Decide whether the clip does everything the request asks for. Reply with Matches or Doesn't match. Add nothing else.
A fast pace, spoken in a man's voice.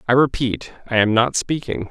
Doesn't match